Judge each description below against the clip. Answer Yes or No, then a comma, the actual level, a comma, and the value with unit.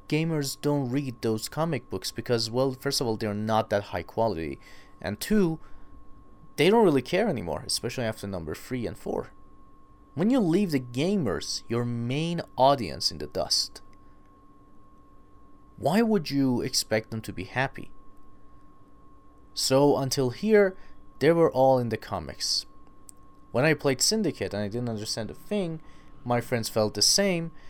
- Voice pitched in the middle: No, low, 120 Hz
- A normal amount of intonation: No, wide, 6.1 semitones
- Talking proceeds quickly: No, average, 155 wpm